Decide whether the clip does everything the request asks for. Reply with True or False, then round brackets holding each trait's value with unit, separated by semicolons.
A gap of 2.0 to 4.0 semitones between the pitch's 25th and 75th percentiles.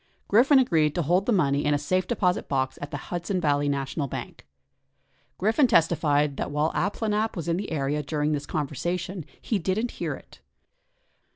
False (5.1 semitones)